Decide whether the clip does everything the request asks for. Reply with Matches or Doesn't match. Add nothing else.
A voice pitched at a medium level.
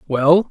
Matches